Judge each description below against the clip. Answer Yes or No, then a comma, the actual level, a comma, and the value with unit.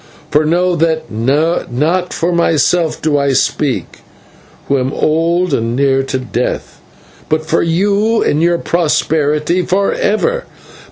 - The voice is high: No, medium, 160 Hz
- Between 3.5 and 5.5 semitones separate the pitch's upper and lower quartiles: Yes, average, 3.8 semitones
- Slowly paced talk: Yes, slow, 130 wpm